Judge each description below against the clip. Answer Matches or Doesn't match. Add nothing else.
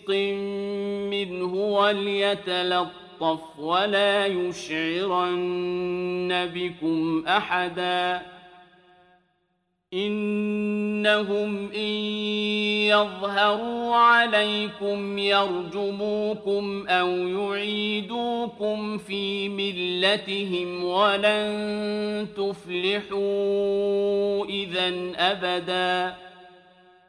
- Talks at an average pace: Doesn't match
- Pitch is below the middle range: Doesn't match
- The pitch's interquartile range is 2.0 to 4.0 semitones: Matches